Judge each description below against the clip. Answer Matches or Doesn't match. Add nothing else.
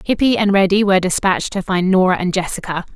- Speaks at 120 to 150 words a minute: Doesn't match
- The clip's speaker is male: Doesn't match